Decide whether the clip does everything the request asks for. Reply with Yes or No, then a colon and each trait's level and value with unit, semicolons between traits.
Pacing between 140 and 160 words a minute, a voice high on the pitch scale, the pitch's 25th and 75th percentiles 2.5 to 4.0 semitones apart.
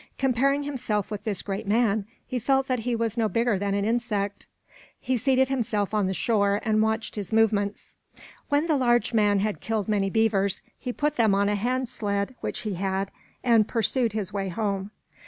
No: average, 195 wpm; high, 220 Hz; average, 3.1 semitones